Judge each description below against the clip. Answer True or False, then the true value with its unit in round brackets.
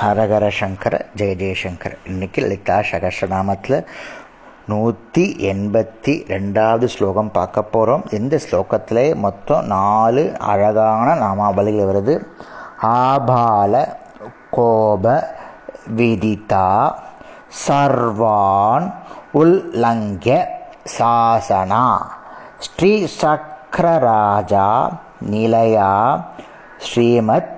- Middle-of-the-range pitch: False (110 Hz)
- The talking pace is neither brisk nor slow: False (65 wpm)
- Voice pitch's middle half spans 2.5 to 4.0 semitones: True (3.0 semitones)